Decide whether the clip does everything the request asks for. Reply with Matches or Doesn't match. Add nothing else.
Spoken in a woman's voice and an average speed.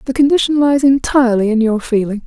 Matches